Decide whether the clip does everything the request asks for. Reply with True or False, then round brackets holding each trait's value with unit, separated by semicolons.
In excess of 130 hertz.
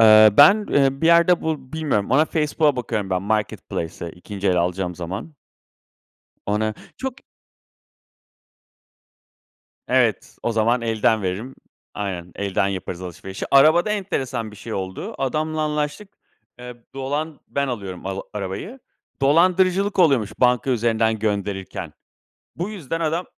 False (120 Hz)